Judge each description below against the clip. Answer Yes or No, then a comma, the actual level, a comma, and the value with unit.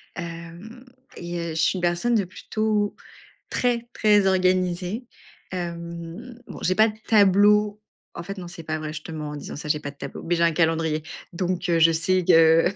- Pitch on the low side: No, medium, 175 Hz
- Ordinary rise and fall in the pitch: Yes, average, 3.7 semitones